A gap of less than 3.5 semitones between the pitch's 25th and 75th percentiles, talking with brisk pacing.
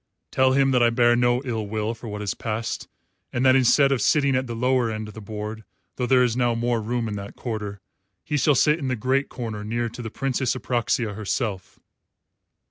Yes: average, 2.9 semitones; fast, 215 wpm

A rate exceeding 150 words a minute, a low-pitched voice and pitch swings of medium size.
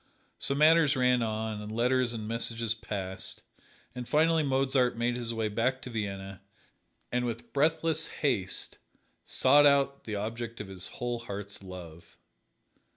No: average, 145 wpm; low, 115 Hz; average, 4.0 semitones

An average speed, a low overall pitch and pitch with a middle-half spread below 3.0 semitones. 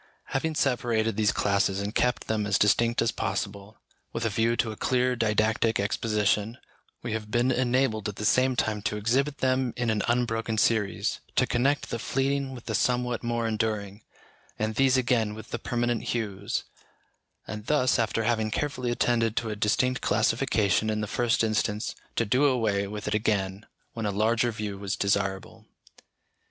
Yes: average, 170 wpm; low, 110 Hz; narrow, 2.6 semitones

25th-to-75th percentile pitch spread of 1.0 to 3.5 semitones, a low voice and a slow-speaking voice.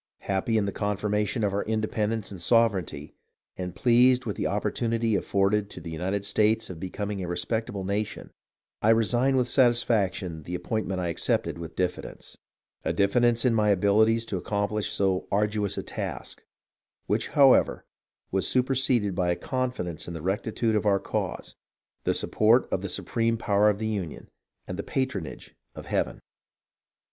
No: average, 3.0 semitones; low, 105 Hz; average, 165 wpm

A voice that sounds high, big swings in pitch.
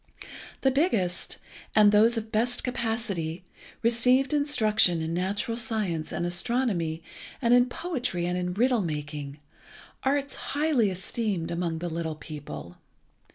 Yes: high, 210 Hz; wide, 6.4 semitones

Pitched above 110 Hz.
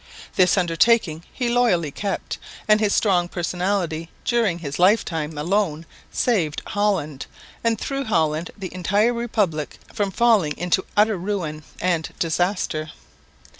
Yes: medium, 185 Hz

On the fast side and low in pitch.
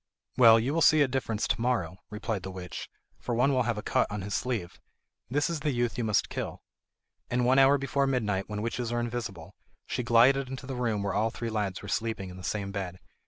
Yes: fast, 230 wpm; low, 115 Hz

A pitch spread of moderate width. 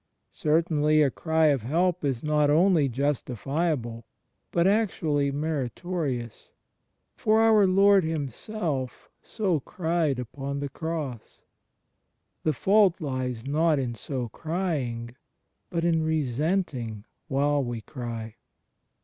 Yes: average, 4.7 semitones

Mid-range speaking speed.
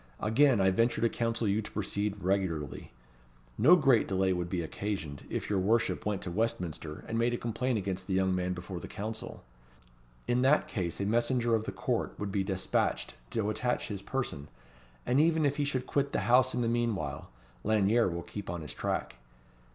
Yes: average, 195 wpm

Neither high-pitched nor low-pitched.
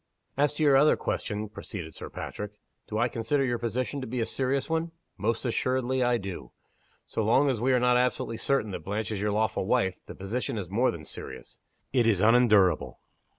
No: low, 115 Hz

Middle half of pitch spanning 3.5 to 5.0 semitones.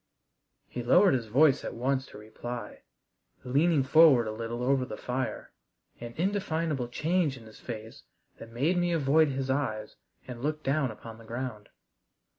Yes: average, 4.6 semitones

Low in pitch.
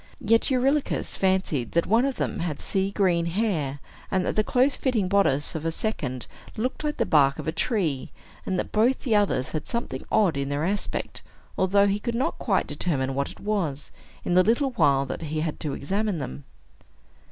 No: high, 190 Hz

